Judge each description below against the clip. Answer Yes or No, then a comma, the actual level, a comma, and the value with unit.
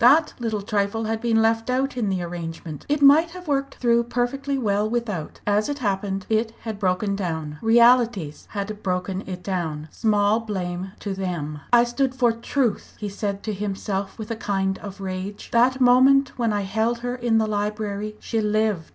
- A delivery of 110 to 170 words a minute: No, average, 185 wpm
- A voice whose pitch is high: Yes, high, 215 Hz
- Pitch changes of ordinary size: Yes, average, 3.7 semitones